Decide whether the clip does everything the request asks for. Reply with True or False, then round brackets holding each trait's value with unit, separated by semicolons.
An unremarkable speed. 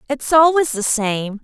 True (165 wpm)